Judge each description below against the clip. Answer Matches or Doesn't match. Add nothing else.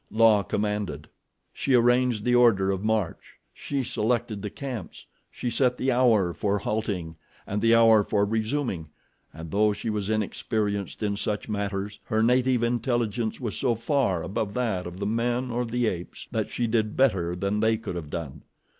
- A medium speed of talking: Matches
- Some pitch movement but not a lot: Matches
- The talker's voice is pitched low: Matches